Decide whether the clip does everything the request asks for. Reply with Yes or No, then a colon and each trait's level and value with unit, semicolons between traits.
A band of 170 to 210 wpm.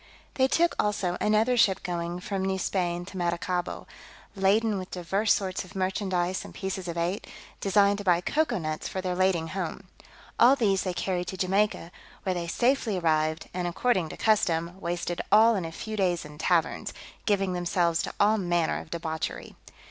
Yes: average, 180 wpm